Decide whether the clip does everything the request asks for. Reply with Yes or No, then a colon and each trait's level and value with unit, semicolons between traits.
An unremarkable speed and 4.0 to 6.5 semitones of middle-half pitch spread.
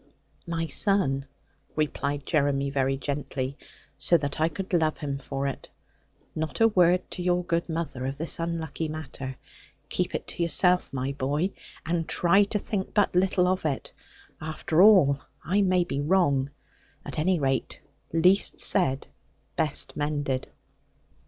Yes: average, 145 wpm; average, 4.3 semitones